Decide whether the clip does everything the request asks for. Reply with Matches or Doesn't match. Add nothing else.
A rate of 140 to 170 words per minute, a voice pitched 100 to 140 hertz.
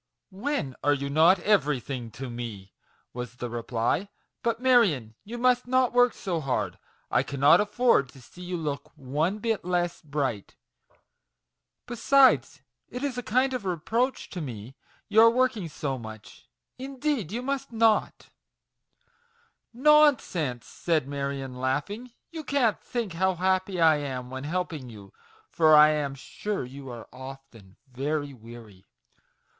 Doesn't match